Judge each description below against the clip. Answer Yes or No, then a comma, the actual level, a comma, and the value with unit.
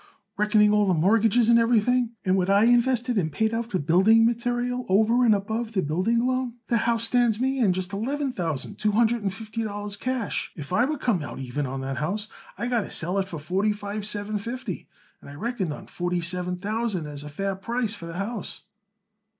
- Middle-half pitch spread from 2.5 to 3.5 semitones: No, average, 4.2 semitones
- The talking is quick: Yes, fast, 215 wpm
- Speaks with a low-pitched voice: No, high, 210 Hz